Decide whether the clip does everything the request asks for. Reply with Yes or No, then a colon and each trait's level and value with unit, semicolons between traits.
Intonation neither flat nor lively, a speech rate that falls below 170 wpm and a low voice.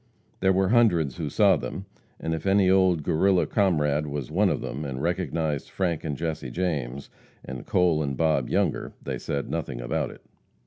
No: average, 4.5 semitones; average, 180 wpm; very low, 80 Hz